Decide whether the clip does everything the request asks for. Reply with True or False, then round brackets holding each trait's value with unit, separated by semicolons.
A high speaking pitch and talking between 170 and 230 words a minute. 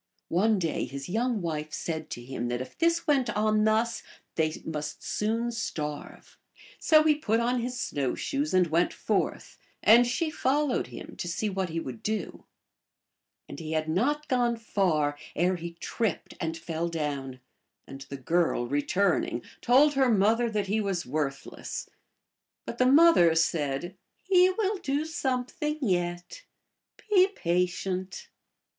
False (195 Hz; 150 wpm)